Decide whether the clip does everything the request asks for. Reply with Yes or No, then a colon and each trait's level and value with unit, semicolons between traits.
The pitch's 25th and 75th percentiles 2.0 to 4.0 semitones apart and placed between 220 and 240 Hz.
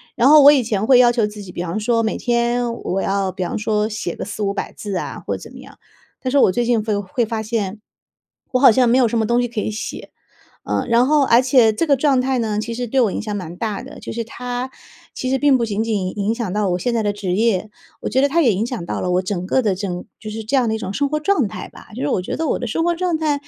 Yes: average, 3.6 semitones; high, 225 Hz